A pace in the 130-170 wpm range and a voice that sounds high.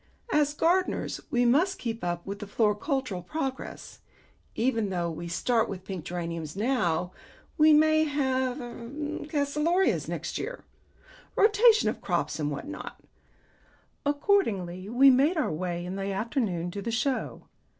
Yes: average, 140 wpm; high, 235 Hz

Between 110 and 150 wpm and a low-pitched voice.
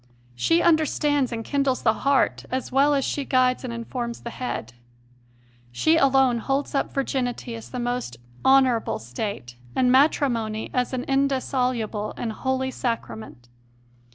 No: average, 140 wpm; very high, 255 Hz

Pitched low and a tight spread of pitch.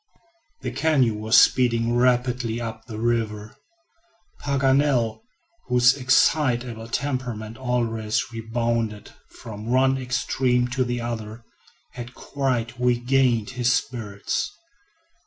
Yes: low, 120 Hz; narrow, 2.1 semitones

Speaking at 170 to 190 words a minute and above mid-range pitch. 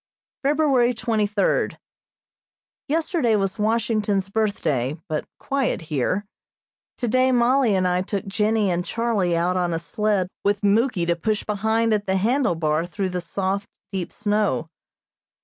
No: average, 140 wpm; high, 205 Hz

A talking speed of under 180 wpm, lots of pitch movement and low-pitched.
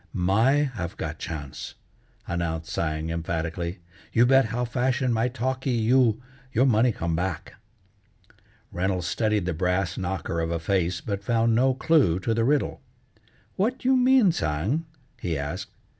Yes: average, 145 wpm; wide, 7.1 semitones; low, 105 Hz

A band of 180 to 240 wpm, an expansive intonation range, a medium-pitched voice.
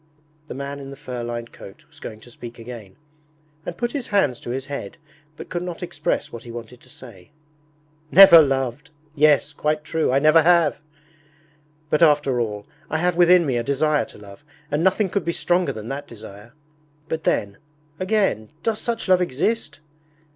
Yes: average, 185 wpm; wide, 6.2 semitones; medium, 145 Hz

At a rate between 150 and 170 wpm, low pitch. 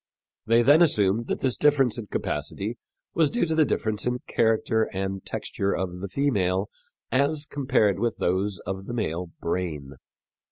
Yes: average, 160 wpm; low, 110 Hz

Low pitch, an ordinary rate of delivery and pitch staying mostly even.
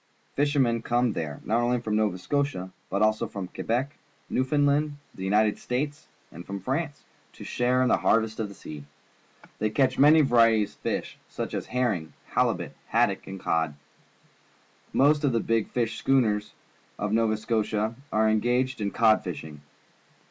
No: low, 115 Hz; average, 160 wpm; average, 3.7 semitones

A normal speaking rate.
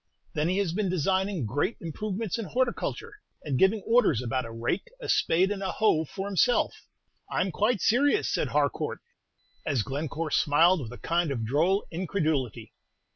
Yes: average, 170 wpm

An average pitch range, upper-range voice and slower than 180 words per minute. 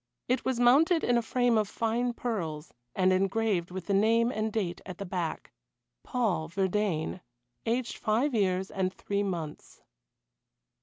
Yes: average, 4.2 semitones; high, 205 Hz; average, 150 wpm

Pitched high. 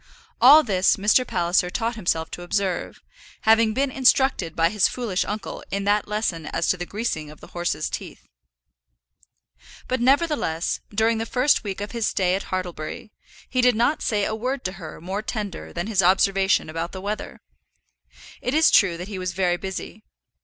Yes: high, 200 Hz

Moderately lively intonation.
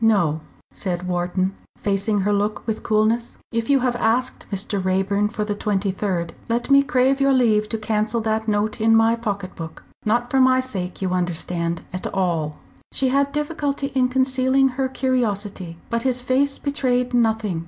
Yes: average, 4.7 semitones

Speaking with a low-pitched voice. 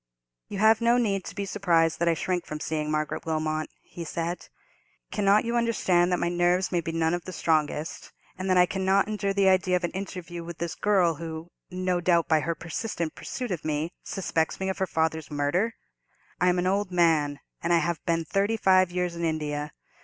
No: medium, 175 Hz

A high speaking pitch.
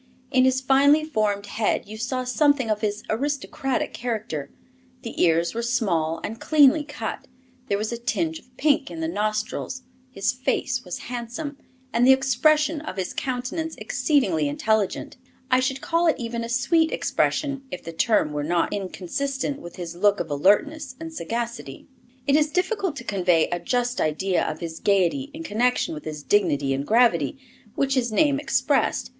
Yes: high, 240 Hz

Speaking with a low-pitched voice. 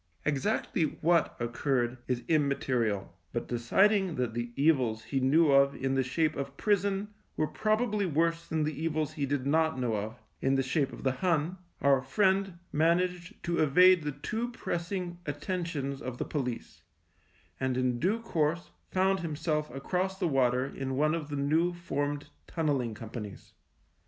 No: medium, 150 Hz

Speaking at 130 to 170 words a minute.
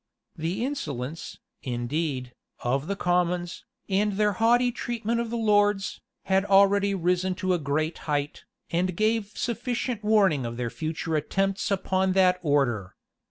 Yes: average, 140 wpm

